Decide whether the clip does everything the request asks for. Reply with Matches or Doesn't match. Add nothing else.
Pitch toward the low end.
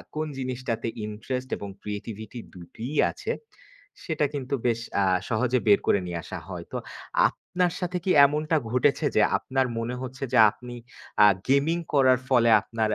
Matches